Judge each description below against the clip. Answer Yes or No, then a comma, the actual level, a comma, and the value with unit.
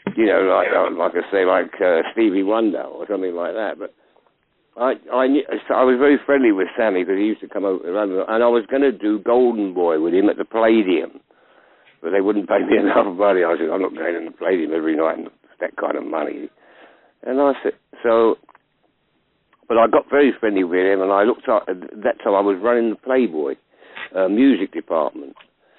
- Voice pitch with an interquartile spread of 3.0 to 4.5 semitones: No, average, 5.0 semitones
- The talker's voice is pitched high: No, low, 120 Hz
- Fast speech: Yes, fast, 215 wpm